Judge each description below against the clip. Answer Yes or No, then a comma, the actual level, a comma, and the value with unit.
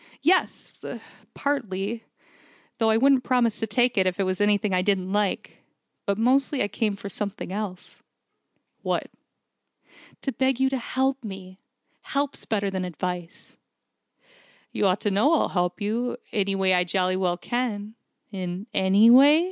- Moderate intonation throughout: Yes, average, 4.6 semitones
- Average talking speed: Yes, average, 160 wpm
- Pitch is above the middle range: Yes, high, 205 Hz